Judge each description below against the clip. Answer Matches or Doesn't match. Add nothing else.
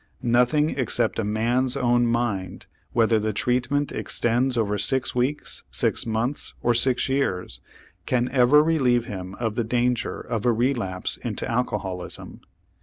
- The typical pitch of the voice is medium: Doesn't match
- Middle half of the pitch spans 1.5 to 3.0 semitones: Matches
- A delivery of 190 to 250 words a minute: Doesn't match